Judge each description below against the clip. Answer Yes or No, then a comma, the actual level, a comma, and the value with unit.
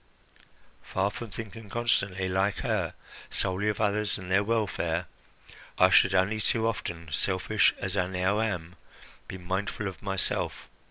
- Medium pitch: No, very low, 95 Hz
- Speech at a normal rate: Yes, average, 145 wpm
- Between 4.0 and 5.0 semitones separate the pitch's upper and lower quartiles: No, narrow, 2.4 semitones